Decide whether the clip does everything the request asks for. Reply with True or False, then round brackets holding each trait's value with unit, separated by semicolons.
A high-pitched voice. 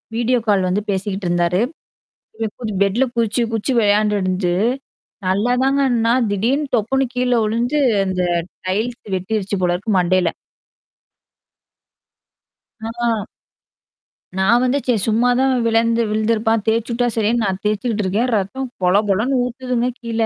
True (225 Hz)